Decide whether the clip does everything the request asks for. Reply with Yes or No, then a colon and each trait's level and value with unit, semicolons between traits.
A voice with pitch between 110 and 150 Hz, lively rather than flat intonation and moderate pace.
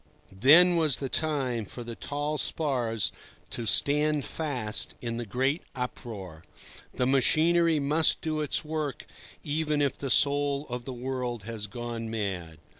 No: low, 135 Hz; average, 4.4 semitones; average, 145 wpm